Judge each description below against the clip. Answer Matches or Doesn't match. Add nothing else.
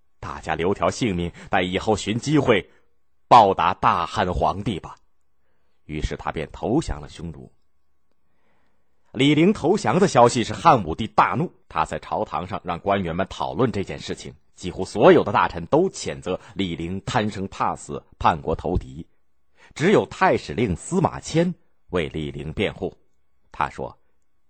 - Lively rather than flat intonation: Matches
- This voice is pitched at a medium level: Doesn't match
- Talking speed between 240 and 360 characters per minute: Doesn't match